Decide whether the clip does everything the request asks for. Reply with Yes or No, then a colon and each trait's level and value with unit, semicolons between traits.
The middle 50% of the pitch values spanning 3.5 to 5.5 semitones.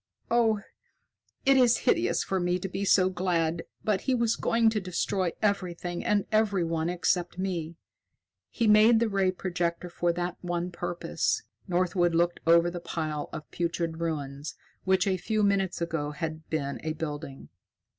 No: average, 2.9 semitones